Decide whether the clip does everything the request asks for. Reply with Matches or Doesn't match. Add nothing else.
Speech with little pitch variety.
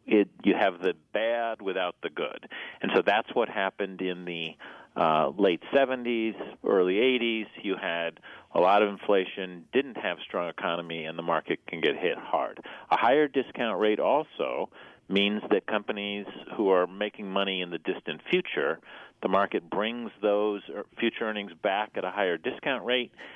Doesn't match